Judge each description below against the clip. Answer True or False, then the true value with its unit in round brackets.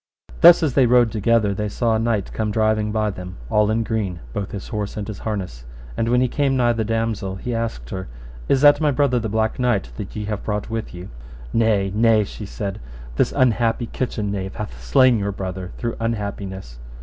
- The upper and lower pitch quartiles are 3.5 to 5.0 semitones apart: False (2.8 semitones)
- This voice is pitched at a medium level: False (110 Hz)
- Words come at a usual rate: False (210 wpm)